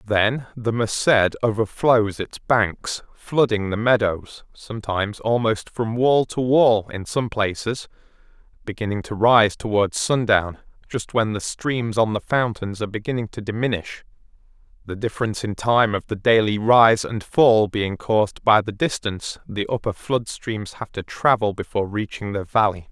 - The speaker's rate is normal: Yes, average, 155 wpm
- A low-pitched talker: Yes, low, 110 Hz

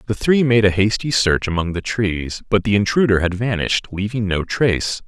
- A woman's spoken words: No, male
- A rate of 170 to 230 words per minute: Yes, average, 200 wpm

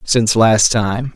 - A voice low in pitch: Yes, low, 115 Hz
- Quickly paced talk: No, average, 155 wpm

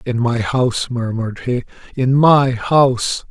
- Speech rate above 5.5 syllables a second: No, 4.3 syllables/s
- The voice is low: Yes, low, 125 Hz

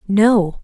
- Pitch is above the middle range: Yes, high, 205 Hz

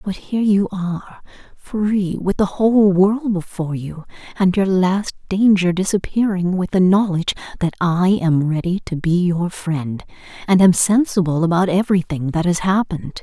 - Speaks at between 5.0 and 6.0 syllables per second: No, 4.8 syllables/s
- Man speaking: No, female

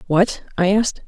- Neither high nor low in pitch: No, high, 195 Hz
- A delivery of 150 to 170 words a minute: Yes, average, 165 wpm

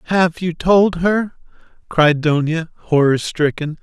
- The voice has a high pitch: No, medium, 165 Hz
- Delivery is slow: Yes, slow, 125 wpm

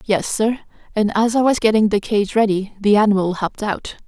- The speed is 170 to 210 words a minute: Yes, fast, 205 wpm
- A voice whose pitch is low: No, high, 210 Hz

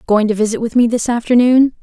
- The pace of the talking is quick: Yes, fast, 230 wpm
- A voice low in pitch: No, high, 230 Hz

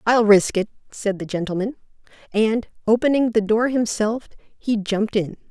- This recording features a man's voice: No, female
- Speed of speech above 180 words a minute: No, average, 155 wpm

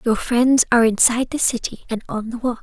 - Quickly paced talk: Yes, fast, 230 wpm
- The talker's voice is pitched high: Yes, high, 235 Hz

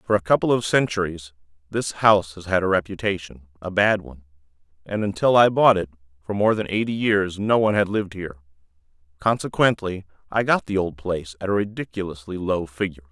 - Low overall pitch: Yes, very low, 95 Hz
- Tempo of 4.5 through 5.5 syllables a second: No, 6.1 syllables/s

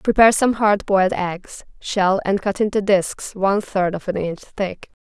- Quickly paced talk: No, average, 190 wpm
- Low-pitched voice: No, high, 195 Hz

